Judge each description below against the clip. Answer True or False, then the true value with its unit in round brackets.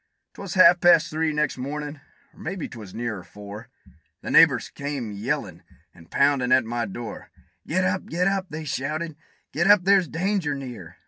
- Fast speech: False (180 wpm)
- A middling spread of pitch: False (6.5 semitones)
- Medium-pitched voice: True (145 Hz)